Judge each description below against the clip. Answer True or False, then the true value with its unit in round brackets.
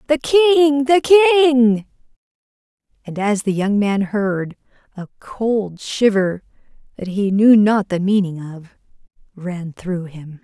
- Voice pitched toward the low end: False (220 Hz)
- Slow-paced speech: True (130 wpm)